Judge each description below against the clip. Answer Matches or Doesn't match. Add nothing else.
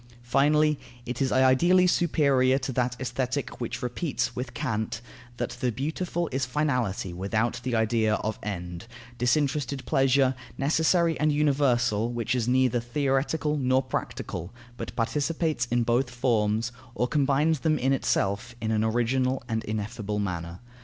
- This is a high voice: Doesn't match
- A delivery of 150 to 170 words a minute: Doesn't match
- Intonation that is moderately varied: Matches